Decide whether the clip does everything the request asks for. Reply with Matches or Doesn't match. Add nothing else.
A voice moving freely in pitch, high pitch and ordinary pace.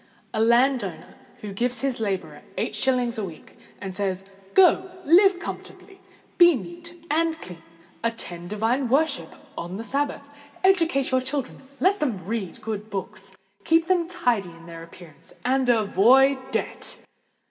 Doesn't match